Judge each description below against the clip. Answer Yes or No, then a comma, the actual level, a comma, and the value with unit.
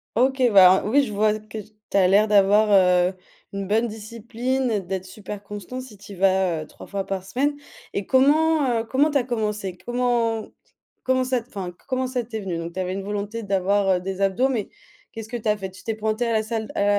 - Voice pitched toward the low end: No, high, 215 Hz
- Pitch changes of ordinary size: Yes, average, 3.8 semitones